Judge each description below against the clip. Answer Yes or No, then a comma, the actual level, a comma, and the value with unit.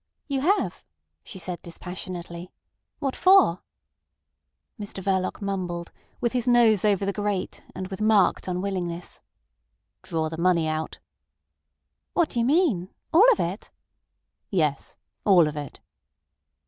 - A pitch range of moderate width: Yes, average, 4.5 semitones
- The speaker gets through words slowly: Yes, slow, 125 wpm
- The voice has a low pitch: No, high, 190 Hz